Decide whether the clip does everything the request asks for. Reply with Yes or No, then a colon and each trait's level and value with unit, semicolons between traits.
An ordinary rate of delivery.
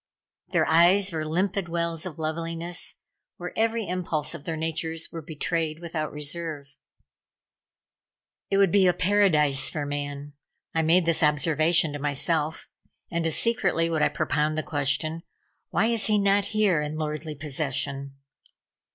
Yes: average, 145 wpm